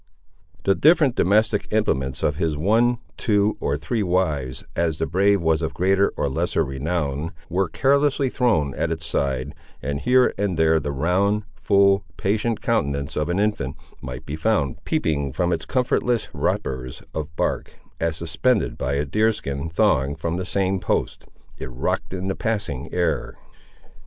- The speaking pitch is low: Yes, very low, 85 Hz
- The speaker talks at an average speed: Yes, average, 160 wpm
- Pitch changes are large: Yes, wide, 6.1 semitones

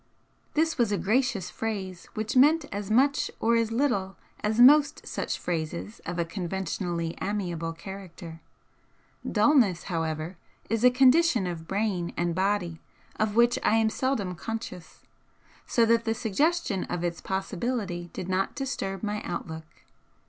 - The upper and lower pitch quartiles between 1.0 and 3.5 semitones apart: No, average, 5.1 semitones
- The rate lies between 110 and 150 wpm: Yes, average, 140 wpm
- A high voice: Yes, high, 205 Hz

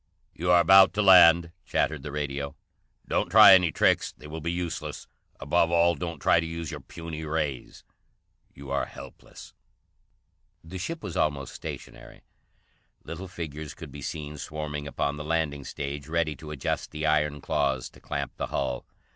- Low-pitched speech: Yes, very low, 75 Hz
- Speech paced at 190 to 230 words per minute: No, average, 165 wpm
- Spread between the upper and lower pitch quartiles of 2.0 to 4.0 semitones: Yes, narrow, 2.6 semitones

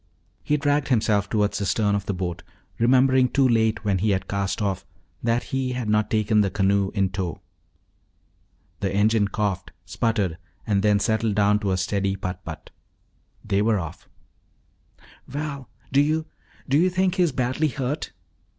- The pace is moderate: Yes, average, 170 wpm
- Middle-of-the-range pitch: No, low, 105 Hz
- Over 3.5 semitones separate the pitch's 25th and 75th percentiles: Yes, average, 4.5 semitones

